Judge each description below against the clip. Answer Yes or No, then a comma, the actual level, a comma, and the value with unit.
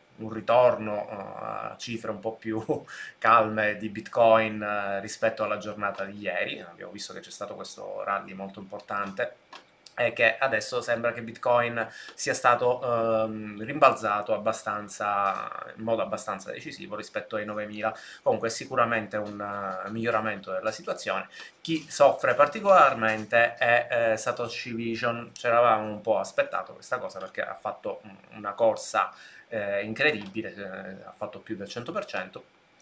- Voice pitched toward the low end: Yes, low, 110 Hz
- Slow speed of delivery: No, average, 135 wpm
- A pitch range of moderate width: No, narrow, 2.0 semitones